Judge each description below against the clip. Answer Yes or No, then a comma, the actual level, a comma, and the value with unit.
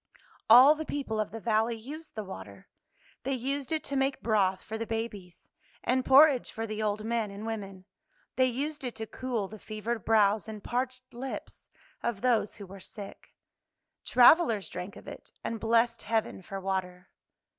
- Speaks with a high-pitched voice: Yes, high, 225 Hz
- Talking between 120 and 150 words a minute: No, average, 175 wpm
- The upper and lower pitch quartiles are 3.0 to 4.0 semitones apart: Yes, average, 3.7 semitones